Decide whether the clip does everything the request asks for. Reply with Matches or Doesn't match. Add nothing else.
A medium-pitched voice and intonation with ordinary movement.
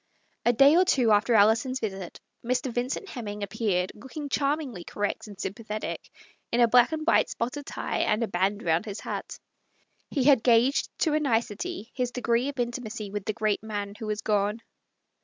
Doesn't match